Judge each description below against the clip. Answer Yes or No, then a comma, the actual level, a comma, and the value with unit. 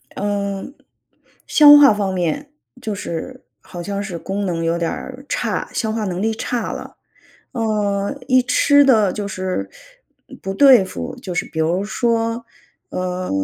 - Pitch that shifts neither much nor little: Yes, average, 4.5 semitones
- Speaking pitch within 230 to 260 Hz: No, high, 205 Hz